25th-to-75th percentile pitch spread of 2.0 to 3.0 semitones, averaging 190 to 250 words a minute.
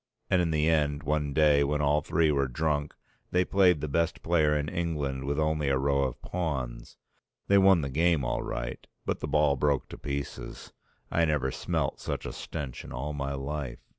Yes: narrow, 2.4 semitones; average, 195 wpm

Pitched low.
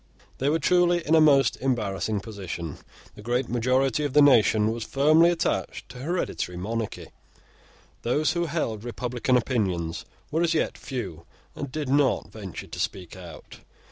Yes: low, 125 Hz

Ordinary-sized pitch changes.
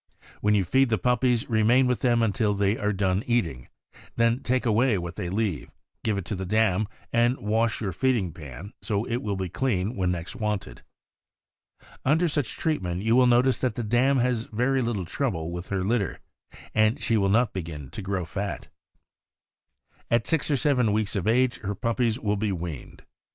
Yes: average, 4.2 semitones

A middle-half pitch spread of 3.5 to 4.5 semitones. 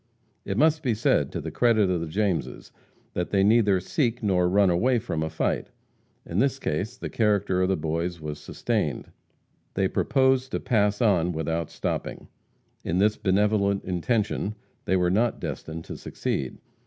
Yes: average, 4.2 semitones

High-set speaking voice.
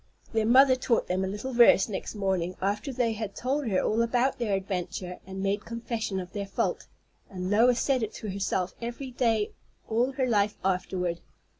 Yes: high, 215 Hz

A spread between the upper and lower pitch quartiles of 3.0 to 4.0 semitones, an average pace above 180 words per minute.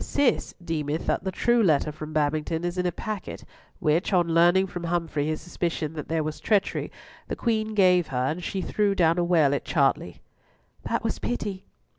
Yes: average, 3.5 semitones; average, 190 wpm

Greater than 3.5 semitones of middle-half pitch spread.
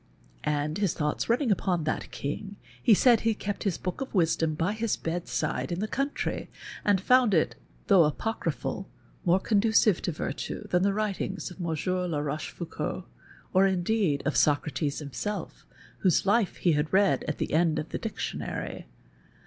Yes: average, 4.8 semitones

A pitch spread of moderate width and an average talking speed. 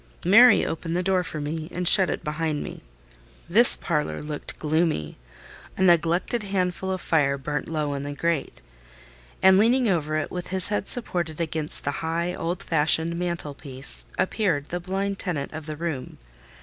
Yes: average, 3.5 semitones; average, 165 wpm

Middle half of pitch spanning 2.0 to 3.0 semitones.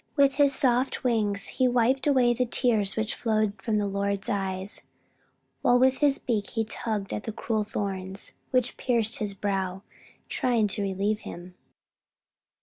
No: average, 3.7 semitones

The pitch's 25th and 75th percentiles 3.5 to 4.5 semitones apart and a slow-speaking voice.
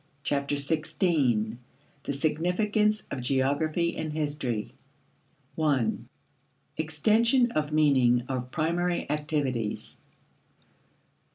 Yes: average, 4.0 semitones; slow, 80 wpm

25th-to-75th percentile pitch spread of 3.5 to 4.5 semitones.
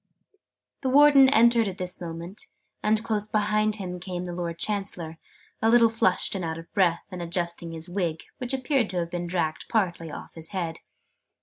Yes: average, 4.1 semitones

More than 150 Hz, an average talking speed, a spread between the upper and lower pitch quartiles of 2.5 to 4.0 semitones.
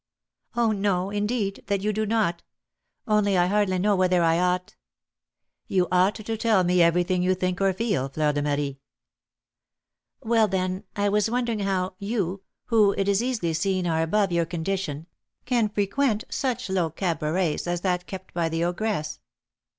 Yes: high, 190 Hz; average, 165 wpm; average, 3.1 semitones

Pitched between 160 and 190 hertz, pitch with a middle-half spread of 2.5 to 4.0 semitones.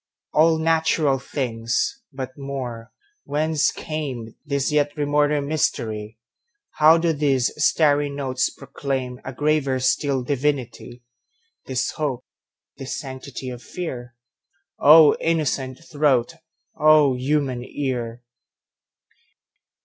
No: medium, 140 Hz; average, 3.1 semitones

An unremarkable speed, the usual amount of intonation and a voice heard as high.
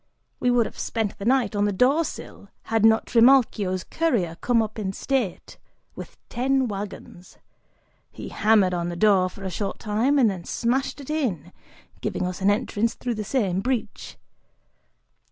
Yes: average, 170 wpm; average, 4.3 semitones; high, 215 Hz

